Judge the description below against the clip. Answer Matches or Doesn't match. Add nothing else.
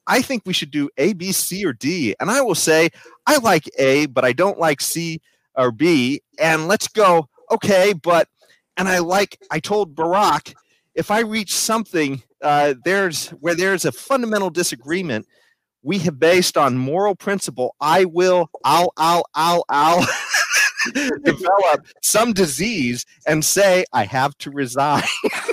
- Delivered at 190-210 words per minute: Doesn't match